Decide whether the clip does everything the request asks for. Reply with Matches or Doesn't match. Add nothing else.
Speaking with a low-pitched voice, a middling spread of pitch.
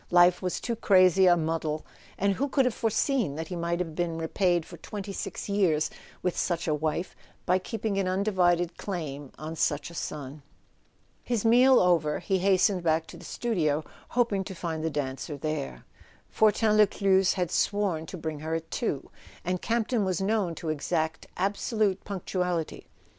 Doesn't match